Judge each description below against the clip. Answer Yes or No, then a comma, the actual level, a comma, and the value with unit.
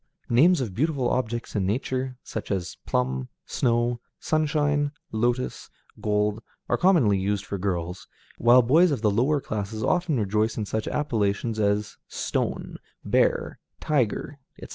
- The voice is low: Yes, low, 115 Hz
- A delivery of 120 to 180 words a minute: Yes, average, 140 wpm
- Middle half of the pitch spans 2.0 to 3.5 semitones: No, average, 5.1 semitones